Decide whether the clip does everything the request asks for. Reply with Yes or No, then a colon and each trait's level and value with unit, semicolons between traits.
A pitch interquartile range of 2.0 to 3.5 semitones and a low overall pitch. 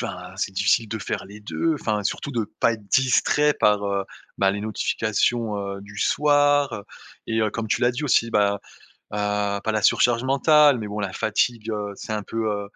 Yes: average, 2.9 semitones; low, 110 Hz